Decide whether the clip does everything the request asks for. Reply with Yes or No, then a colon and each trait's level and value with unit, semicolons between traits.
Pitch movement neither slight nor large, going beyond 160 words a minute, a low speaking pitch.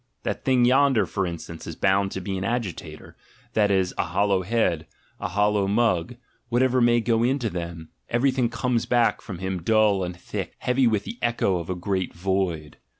Yes: average, 4.6 semitones; average, 185 wpm; low, 100 Hz